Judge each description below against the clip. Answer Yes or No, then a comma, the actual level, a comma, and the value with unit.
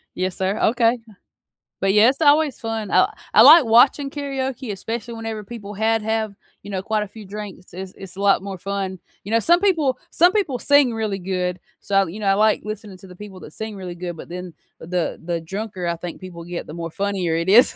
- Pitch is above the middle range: Yes, high, 205 Hz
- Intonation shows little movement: No, average, 3.6 semitones